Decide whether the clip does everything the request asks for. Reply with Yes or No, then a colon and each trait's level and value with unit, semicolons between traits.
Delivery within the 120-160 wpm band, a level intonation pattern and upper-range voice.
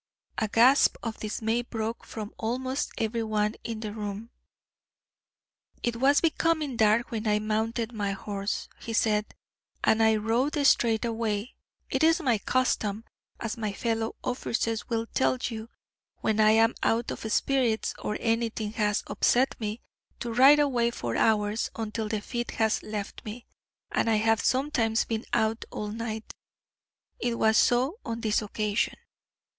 Yes: average, 150 wpm; narrow, 1.9 semitones; high, 225 Hz